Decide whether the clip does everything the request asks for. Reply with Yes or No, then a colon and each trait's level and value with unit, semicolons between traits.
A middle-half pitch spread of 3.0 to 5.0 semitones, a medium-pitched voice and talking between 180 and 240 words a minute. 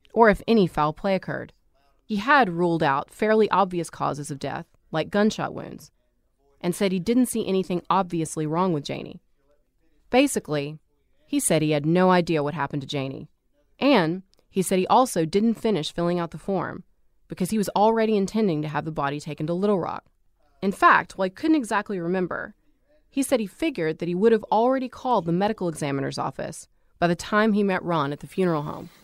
No: wide, 5.4 semitones; medium, 180 Hz; average, 195 wpm